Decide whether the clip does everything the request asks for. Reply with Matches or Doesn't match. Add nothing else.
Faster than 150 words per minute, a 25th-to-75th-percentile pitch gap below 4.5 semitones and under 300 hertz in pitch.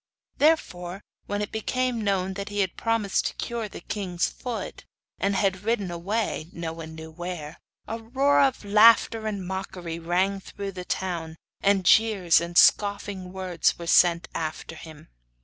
Matches